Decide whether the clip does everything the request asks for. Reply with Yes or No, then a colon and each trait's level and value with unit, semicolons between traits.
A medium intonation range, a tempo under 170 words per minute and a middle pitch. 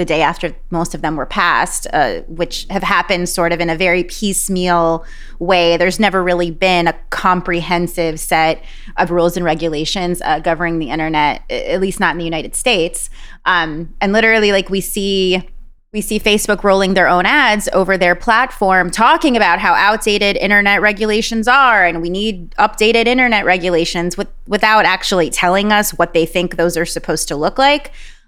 No: average, 3.3 semitones; average, 180 wpm; medium, 180 Hz